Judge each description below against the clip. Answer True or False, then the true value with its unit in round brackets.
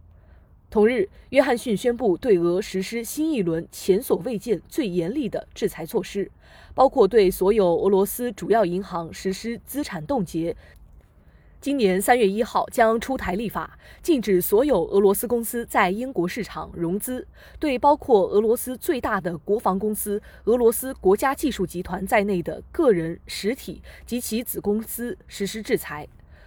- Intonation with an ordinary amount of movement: True (5.0 semitones)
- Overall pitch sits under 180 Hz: False (205 Hz)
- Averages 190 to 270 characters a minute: True (245 characters per minute)